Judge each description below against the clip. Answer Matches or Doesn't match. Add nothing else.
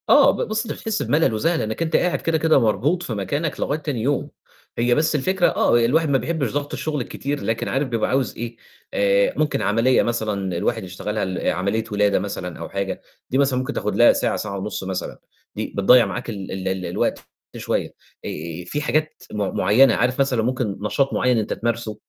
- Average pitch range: Doesn't match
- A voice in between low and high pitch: Doesn't match